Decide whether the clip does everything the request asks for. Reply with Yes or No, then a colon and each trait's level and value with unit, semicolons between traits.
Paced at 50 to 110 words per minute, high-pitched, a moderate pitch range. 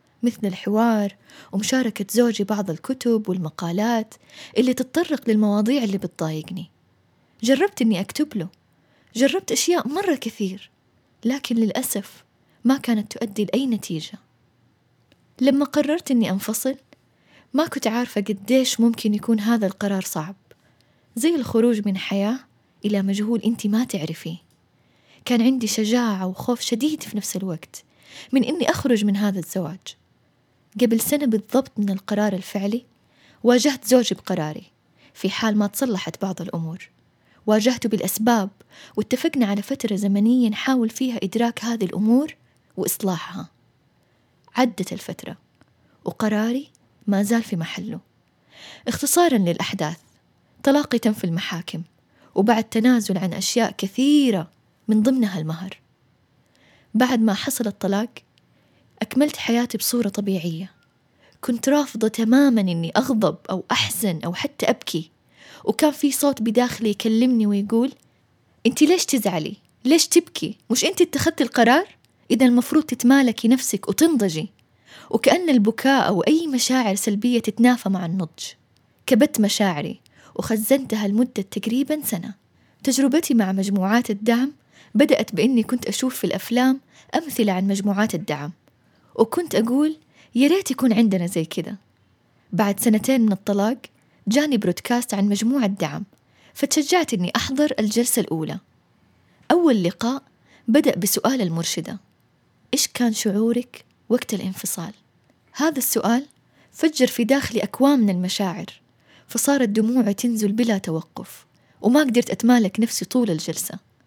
No: average, 120 wpm; high, 225 Hz; average, 4.4 semitones